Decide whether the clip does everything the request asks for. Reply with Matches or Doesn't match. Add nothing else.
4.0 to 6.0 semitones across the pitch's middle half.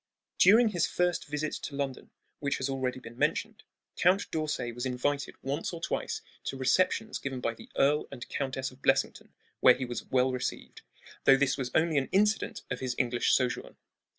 Doesn't match